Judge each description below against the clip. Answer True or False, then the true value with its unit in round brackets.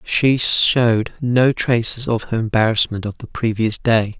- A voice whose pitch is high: False (115 Hz)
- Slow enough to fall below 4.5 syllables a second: True (4.2 syllables/s)